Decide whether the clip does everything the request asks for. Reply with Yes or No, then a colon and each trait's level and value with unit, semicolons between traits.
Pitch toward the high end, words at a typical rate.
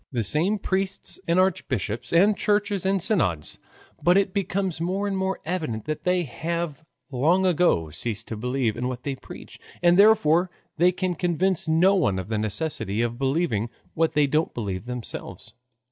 No: medium, 165 Hz; average, 170 wpm